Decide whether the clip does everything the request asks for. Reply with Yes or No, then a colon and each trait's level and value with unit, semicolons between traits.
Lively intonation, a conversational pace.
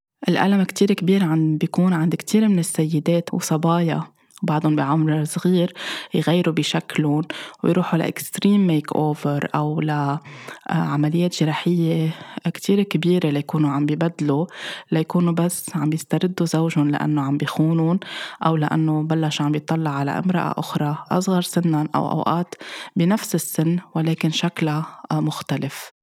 No: narrow, 2.5 semitones; average, 120 wpm